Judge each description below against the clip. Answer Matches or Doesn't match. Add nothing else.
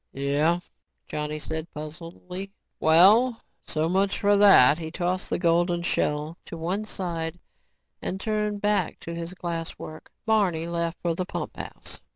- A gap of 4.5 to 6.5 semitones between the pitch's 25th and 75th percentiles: Doesn't match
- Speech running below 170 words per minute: Matches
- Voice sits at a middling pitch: Matches